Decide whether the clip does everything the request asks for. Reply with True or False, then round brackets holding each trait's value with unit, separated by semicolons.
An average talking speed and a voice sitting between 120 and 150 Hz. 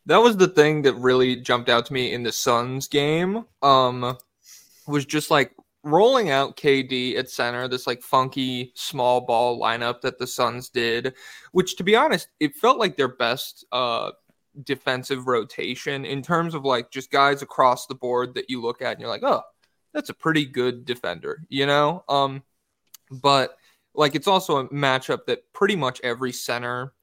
True (180 wpm; 135 Hz)